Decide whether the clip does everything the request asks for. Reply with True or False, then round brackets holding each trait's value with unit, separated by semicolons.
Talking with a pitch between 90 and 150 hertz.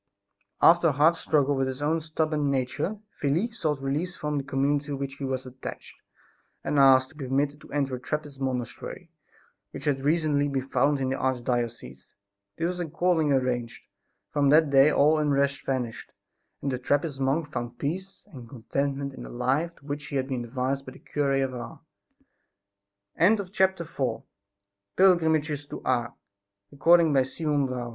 True (140 Hz)